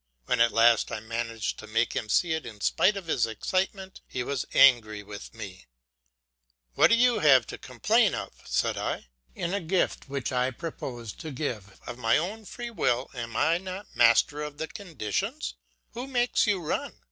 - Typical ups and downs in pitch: No, wide, 8.4 semitones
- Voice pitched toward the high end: No, low, 135 Hz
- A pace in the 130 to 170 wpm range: No, average, 180 wpm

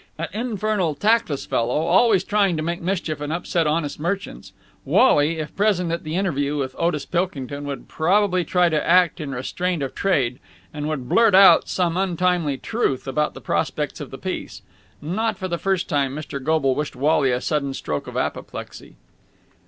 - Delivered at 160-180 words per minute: Yes, average, 175 wpm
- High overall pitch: No, medium, 165 Hz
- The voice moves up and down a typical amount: Yes, average, 4.3 semitones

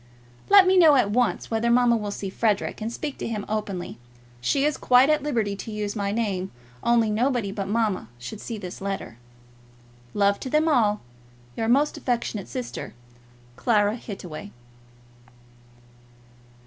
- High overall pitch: Yes, high, 220 Hz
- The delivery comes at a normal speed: Yes, average, 150 wpm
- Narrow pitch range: No, average, 3.6 semitones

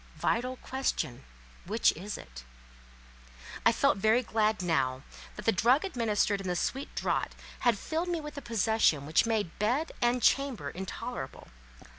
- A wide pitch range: Yes, wide, 6.2 semitones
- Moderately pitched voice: No, high, 220 Hz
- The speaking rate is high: No, average, 145 wpm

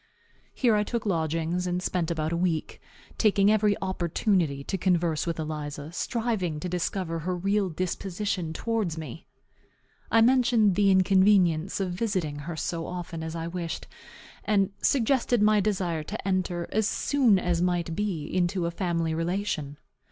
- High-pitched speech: No, medium, 180 Hz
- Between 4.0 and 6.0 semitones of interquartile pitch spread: No, average, 3.6 semitones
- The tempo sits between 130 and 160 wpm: Yes, average, 150 wpm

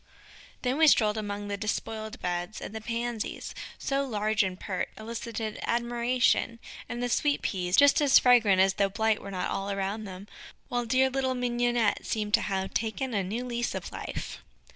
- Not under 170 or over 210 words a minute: Yes, average, 180 wpm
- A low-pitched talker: No, high, 220 Hz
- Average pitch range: Yes, average, 3.2 semitones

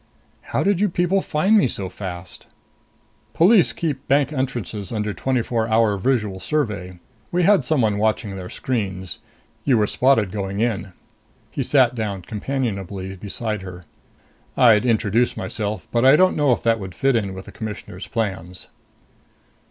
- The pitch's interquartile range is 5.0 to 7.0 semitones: Yes, wide, 5.4 semitones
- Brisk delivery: No, average, 155 wpm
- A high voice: No, low, 110 Hz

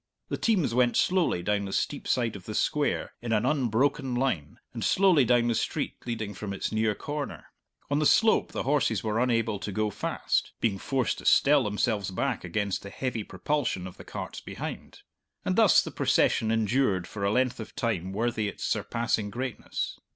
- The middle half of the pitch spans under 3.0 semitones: No, average, 4.2 semitones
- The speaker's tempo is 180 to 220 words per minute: Yes, average, 190 wpm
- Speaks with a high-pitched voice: No, low, 115 Hz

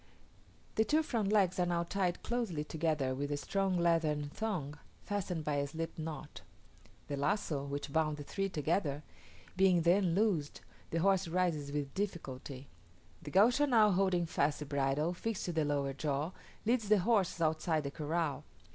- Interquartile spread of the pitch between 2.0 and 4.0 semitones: No, average, 4.9 semitones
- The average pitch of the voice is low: No, medium, 165 Hz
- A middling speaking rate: Yes, average, 165 wpm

